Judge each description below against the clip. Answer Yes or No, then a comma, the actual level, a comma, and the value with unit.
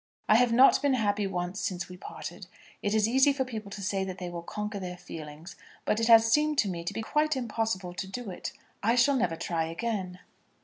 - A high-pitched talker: Yes, high, 210 Hz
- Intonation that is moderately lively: Yes, average, 4.5 semitones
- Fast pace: Yes, fast, 225 wpm